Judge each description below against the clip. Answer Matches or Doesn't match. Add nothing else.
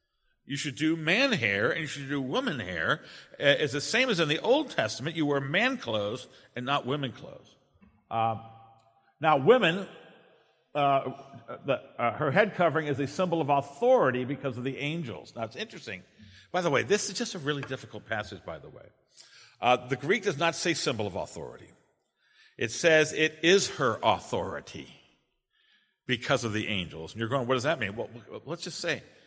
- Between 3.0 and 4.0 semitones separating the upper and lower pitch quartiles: Doesn't match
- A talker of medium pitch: Matches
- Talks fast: Doesn't match